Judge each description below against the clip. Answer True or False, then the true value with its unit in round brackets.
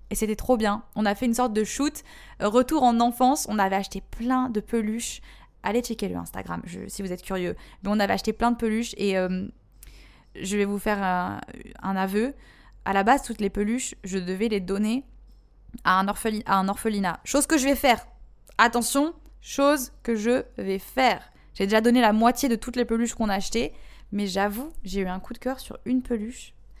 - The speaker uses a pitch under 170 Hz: False (220 Hz)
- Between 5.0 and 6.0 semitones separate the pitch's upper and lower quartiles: False (3.8 semitones)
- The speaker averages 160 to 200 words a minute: False (215 wpm)